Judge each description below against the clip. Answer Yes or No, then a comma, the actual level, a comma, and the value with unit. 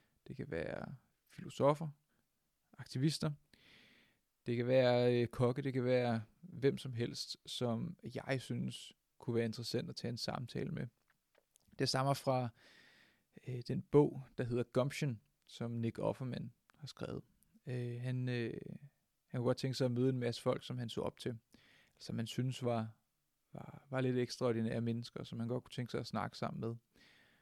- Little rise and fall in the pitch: Yes, narrow, 2.1 semitones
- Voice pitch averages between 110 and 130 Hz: Yes, low, 125 Hz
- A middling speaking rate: Yes, average, 170 wpm